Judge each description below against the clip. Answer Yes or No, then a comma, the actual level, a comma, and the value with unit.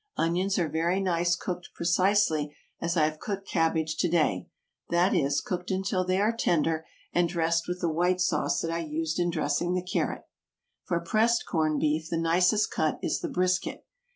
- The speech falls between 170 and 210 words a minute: Yes, average, 180 wpm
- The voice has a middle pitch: Yes, medium, 170 Hz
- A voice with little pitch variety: Yes, narrow, 2.2 semitones